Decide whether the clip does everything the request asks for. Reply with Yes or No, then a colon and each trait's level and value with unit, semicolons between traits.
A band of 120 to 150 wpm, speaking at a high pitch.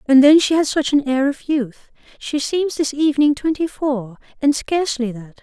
No: average, 200 wpm; very high, 280 Hz